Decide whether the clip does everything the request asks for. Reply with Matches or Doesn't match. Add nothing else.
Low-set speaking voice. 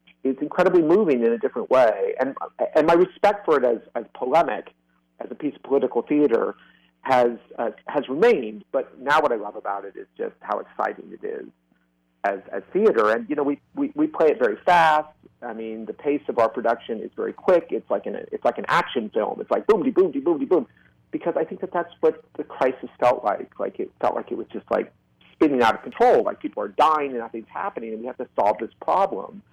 Doesn't match